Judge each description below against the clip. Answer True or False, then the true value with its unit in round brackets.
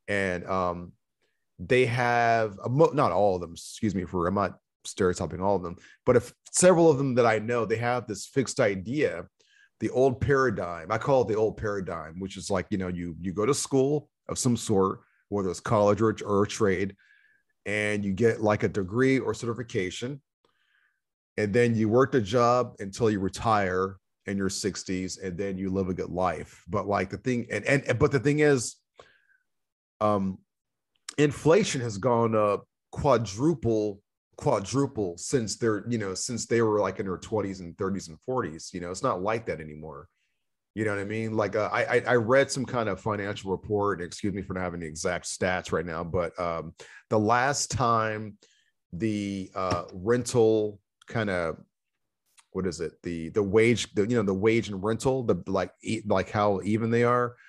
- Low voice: True (105 Hz)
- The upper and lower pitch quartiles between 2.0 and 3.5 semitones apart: False (4.0 semitones)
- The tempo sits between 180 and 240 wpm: True (190 wpm)